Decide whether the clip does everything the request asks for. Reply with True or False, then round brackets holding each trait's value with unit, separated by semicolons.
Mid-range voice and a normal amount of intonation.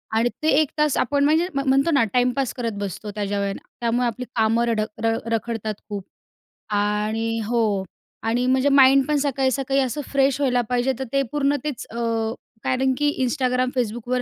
False (250 Hz; 3.3 semitones)